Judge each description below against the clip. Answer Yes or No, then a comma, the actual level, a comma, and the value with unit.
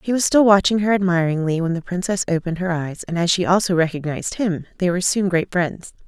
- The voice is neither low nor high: Yes, medium, 180 Hz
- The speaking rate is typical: No, fast, 225 wpm